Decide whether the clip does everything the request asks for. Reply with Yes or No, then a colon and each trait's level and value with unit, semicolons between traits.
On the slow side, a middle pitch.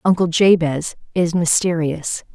Yes: slow, 100 wpm; medium, 170 Hz